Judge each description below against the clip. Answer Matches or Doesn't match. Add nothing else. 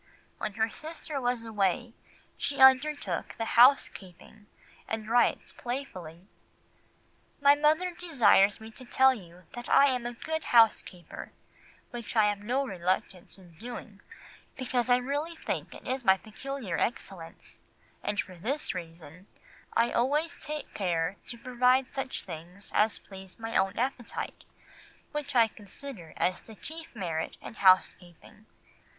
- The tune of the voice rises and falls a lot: Matches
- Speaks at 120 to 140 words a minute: Matches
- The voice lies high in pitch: Matches